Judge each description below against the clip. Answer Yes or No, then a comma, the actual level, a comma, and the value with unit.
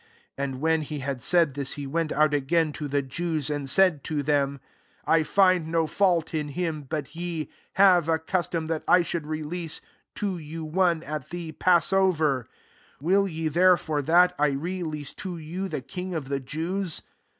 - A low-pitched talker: No, medium, 160 Hz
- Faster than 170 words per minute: Yes, average, 185 wpm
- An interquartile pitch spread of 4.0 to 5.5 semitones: No, average, 3.0 semitones